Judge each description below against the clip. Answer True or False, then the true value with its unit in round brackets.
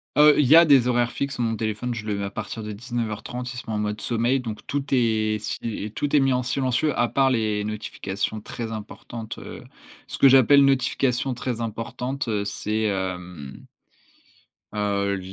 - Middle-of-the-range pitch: False (115 Hz)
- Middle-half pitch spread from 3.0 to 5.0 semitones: True (3.4 semitones)